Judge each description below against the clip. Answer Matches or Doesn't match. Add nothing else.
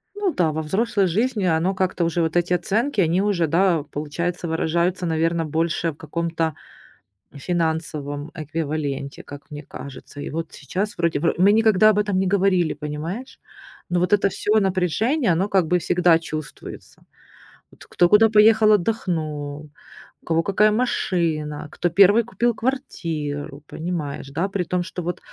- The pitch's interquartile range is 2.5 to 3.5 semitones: Doesn't match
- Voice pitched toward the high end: Doesn't match